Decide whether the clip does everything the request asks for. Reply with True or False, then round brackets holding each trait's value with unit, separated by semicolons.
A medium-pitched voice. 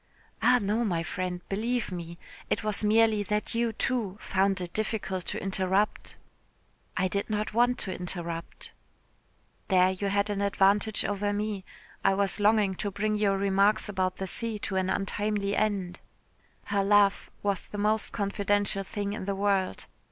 False (200 Hz)